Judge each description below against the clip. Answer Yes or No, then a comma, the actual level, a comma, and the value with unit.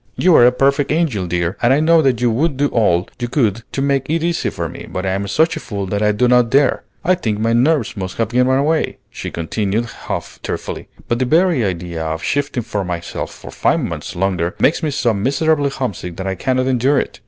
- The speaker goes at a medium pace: No, fast, 235 wpm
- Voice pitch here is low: Yes, low, 125 Hz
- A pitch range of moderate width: No, wide, 6.4 semitones